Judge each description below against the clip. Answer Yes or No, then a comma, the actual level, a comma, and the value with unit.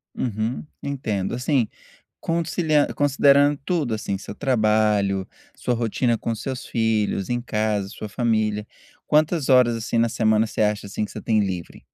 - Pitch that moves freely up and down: No, average, 3.6 semitones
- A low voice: Yes, low, 115 Hz